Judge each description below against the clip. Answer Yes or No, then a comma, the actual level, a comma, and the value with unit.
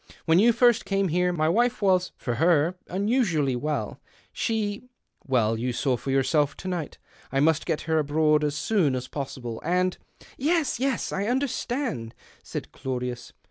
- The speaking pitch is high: No, medium, 160 Hz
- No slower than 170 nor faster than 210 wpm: Yes, average, 185 wpm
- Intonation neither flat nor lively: No, wide, 7.1 semitones